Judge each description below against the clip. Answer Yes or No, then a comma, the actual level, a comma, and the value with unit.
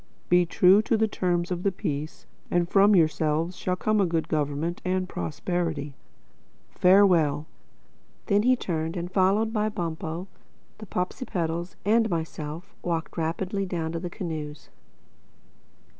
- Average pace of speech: No, slow, 130 wpm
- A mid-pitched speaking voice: Yes, medium, 175 Hz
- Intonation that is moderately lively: Yes, average, 3.4 semitones